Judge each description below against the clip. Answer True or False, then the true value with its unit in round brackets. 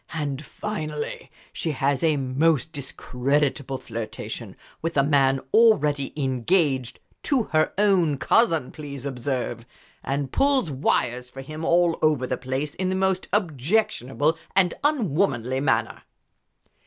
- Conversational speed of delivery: False (125 wpm)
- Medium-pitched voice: True (145 Hz)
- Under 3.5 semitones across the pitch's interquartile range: False (4.3 semitones)